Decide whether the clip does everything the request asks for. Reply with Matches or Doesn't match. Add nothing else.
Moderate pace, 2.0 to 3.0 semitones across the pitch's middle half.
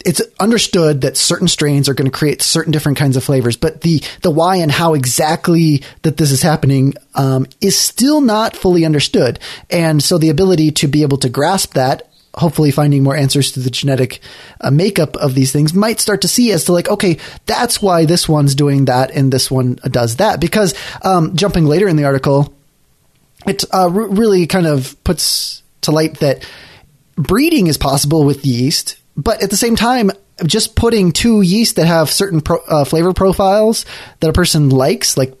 Doesn't match